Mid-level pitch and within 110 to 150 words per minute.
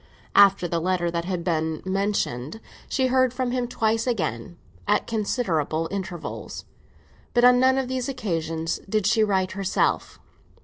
No: high, 195 Hz; average, 145 wpm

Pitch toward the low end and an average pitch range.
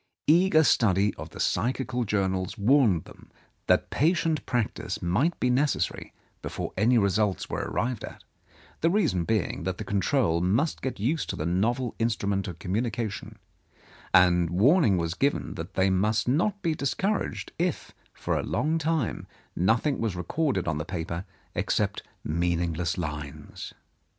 No: low, 105 Hz; wide, 7.4 semitones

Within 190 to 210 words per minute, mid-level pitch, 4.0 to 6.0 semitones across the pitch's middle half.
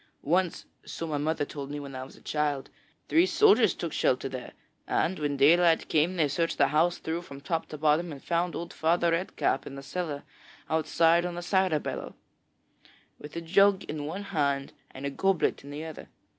No: average, 200 wpm; medium, 160 Hz; average, 3.3 semitones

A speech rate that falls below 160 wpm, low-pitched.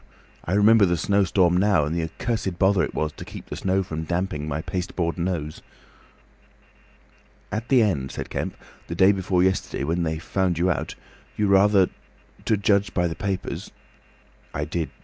No: average, 170 wpm; very low, 95 Hz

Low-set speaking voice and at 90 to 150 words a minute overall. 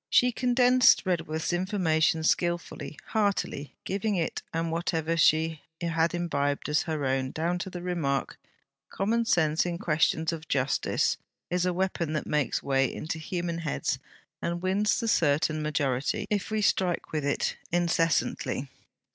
No: medium, 165 Hz; average, 145 wpm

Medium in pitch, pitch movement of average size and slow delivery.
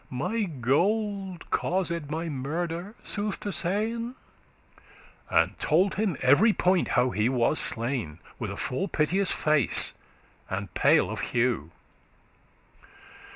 No: medium, 165 Hz; wide, 7.4 semitones; slow, 120 wpm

